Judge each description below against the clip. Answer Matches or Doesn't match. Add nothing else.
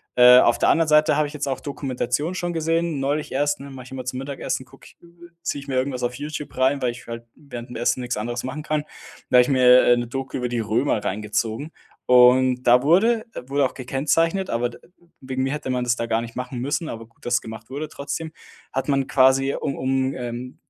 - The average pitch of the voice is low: Matches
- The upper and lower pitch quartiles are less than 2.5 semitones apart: Doesn't match